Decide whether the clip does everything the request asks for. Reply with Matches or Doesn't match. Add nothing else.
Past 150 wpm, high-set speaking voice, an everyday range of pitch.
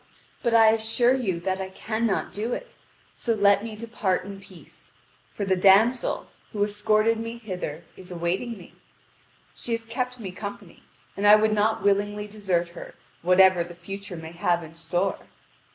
Matches